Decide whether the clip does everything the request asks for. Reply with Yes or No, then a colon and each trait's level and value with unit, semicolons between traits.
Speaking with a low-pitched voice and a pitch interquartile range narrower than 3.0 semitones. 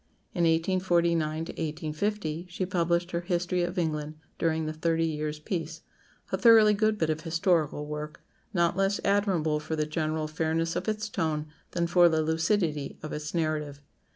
No: medium, 165 Hz; narrow, 2.5 semitones